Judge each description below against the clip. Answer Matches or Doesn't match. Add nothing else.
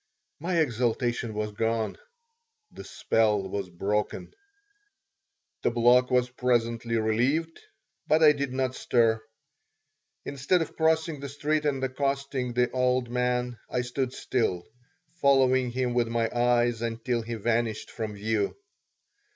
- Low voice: Matches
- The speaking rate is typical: Doesn't match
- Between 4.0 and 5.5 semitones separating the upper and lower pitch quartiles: Doesn't match